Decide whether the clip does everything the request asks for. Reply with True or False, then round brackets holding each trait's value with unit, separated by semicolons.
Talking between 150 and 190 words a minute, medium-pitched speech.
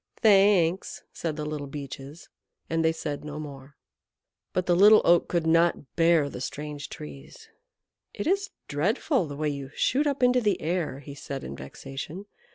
True (165 wpm; 160 Hz)